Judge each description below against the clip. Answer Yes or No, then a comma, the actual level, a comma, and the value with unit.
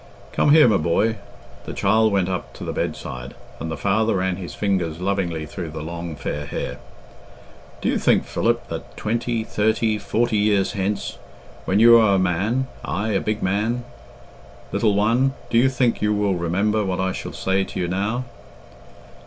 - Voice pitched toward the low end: Yes, low, 100 Hz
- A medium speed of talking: Yes, average, 180 wpm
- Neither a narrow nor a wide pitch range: Yes, average, 3.3 semitones